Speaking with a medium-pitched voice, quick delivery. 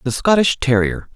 No: medium, 145 Hz; average, 155 wpm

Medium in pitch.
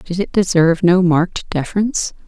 Yes: medium, 175 Hz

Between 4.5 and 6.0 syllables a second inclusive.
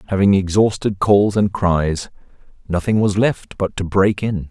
No: 4.3 syllables/s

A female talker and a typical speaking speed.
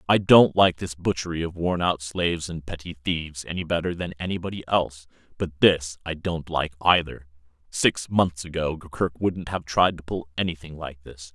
No: male; average, 185 wpm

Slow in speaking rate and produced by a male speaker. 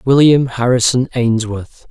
Yes: slow, 95 wpm; male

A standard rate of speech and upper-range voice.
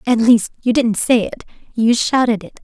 Yes: average, 160 wpm; high, 230 Hz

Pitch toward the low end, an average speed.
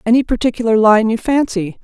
No: high, 225 Hz; average, 165 wpm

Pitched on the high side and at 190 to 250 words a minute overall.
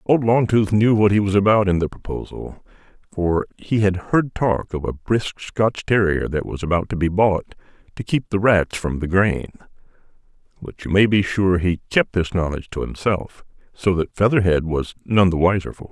No: very low, 95 Hz; average, 200 wpm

